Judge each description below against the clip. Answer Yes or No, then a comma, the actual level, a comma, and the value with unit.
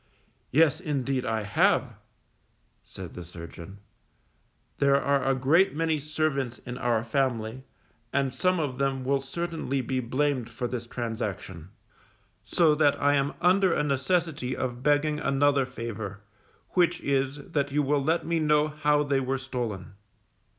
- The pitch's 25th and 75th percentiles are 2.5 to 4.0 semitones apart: Yes, average, 3.3 semitones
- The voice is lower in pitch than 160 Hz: Yes, low, 135 Hz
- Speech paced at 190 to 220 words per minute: No, average, 145 wpm